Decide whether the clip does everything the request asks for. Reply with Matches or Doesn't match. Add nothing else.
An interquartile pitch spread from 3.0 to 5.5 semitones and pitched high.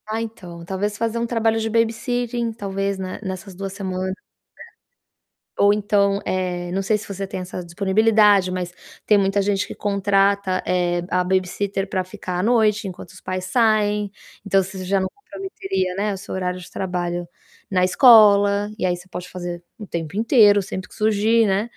Doesn't match